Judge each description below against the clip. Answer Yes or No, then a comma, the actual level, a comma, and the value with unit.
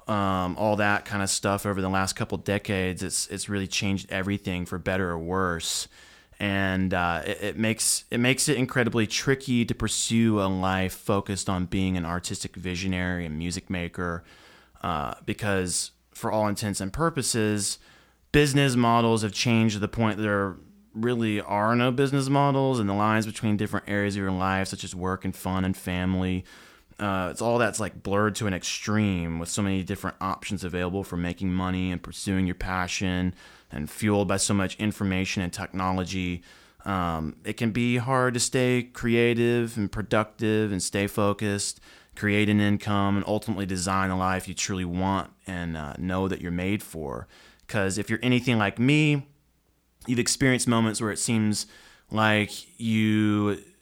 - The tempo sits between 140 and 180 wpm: Yes, average, 170 wpm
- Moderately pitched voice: No, low, 100 Hz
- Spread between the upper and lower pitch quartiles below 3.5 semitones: Yes, average, 2.9 semitones